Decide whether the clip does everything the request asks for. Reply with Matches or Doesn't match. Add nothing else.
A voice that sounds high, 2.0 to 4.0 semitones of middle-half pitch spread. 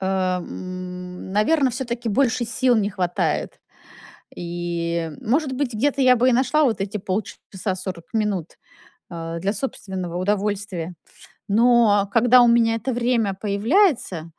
Doesn't match